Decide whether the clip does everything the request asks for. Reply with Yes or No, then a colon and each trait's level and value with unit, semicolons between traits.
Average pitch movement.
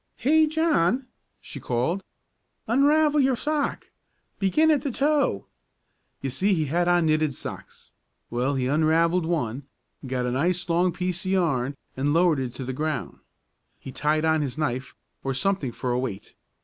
No: wide, 6.6 semitones